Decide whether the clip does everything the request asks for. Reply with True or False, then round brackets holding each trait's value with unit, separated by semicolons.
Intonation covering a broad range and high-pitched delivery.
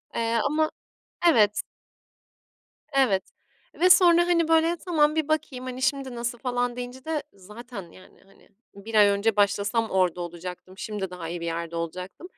True (6.8 semitones; 230 Hz)